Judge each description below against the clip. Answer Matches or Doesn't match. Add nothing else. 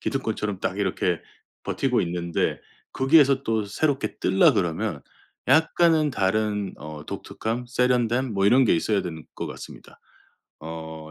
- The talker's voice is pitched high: Doesn't match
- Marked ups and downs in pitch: Matches